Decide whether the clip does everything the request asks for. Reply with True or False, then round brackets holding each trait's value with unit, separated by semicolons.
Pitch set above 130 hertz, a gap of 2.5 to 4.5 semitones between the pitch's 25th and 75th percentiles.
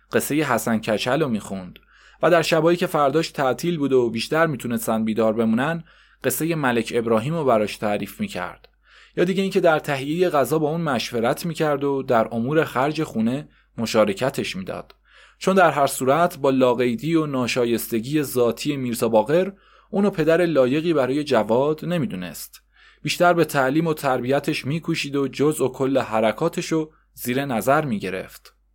False (140 Hz; 5.6 semitones)